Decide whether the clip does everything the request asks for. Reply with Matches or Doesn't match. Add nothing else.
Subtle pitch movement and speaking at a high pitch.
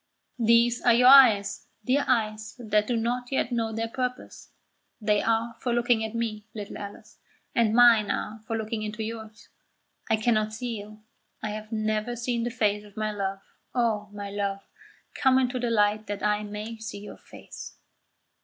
Matches